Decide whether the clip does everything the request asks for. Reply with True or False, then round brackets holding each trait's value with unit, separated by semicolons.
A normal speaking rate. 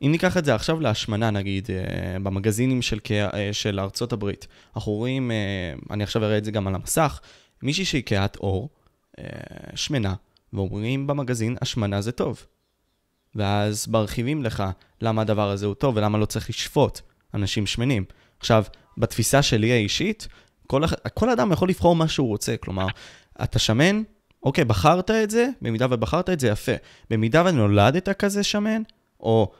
False (160 wpm)